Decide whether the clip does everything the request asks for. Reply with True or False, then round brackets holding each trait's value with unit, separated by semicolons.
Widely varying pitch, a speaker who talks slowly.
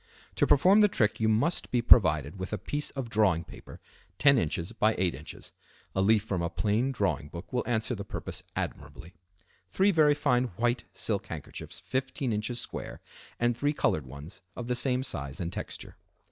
False (6.1 semitones; 185 wpm)